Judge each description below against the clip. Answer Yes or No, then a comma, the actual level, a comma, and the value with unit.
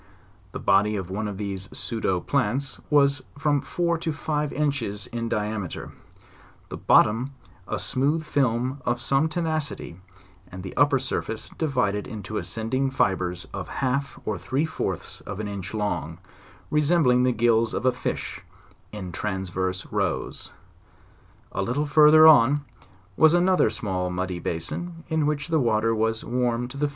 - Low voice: Yes, low, 120 Hz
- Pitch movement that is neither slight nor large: No, wide, 5.9 semitones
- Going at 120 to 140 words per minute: No, average, 150 wpm